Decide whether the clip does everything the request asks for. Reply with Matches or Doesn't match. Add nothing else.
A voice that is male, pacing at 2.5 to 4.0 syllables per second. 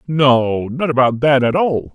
Matches